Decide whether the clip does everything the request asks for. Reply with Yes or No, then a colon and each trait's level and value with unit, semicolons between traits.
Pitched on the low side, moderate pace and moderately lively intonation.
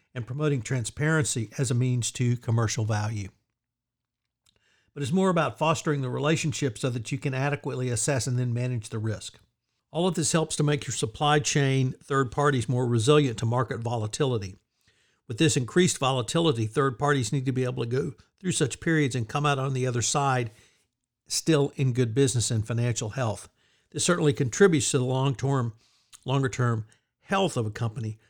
Yes: low, 130 Hz; average, 180 wpm; average, 3.6 semitones